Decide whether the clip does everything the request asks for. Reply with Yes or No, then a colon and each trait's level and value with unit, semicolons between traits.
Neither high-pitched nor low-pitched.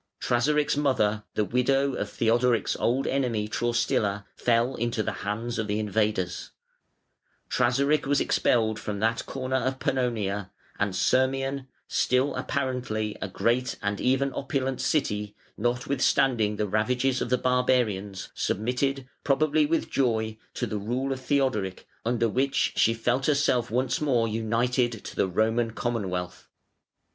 No: low, 120 Hz